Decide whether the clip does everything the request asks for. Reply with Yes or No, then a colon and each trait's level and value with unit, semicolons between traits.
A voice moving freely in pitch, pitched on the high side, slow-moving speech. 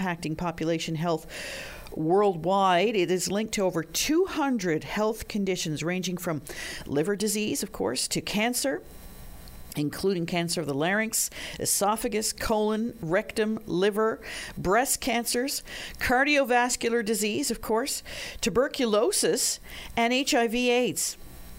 Yes: wide, 5.8 semitones; high, 210 Hz; slow, 110 wpm